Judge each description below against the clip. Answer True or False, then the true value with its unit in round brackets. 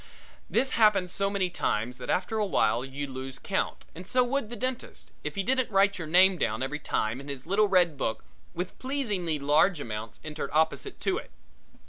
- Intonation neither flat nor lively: False (7.1 semitones)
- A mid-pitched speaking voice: True (180 Hz)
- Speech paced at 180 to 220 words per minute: True (190 wpm)